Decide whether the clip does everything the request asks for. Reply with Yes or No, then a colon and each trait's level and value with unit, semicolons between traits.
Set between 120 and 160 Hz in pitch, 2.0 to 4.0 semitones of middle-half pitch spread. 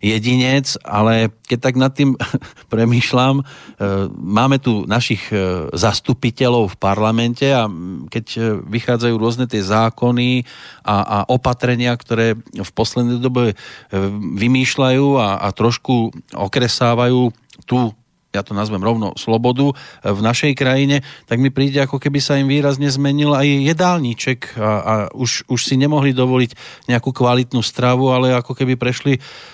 Yes: low, 125 Hz; average, 2.9 semitones